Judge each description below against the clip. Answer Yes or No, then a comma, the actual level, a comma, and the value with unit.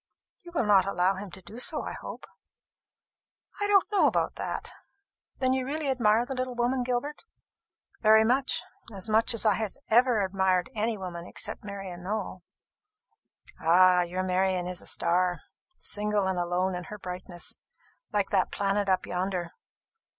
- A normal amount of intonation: Yes, average, 4.6 semitones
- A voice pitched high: Yes, high, 200 Hz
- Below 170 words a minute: Yes, average, 160 wpm